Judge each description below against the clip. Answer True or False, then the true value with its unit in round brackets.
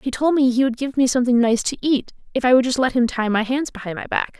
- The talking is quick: True (315 wpm)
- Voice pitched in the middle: False (250 Hz)